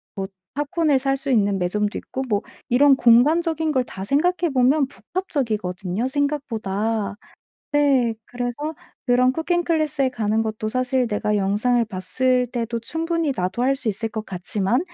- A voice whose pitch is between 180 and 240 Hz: No, very high, 250 Hz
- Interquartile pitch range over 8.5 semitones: No, average, 5.1 semitones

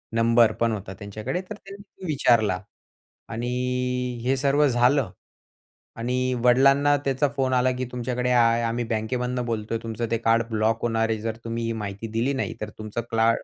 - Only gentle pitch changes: Yes, narrow, 2.3 semitones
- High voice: No, low, 120 Hz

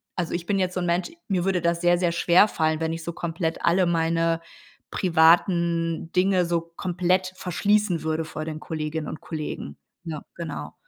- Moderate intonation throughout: No, narrow, 1.9 semitones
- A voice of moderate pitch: Yes, medium, 170 Hz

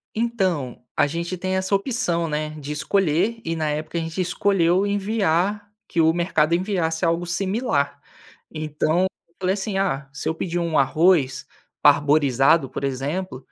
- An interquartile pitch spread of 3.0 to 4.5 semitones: Yes, average, 3.9 semitones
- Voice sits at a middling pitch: Yes, medium, 170 Hz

